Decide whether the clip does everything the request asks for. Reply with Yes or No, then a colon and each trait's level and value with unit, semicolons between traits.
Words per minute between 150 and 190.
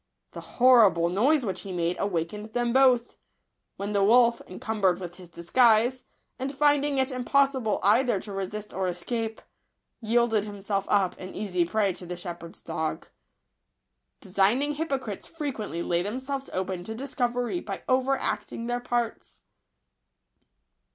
No: average, 140 wpm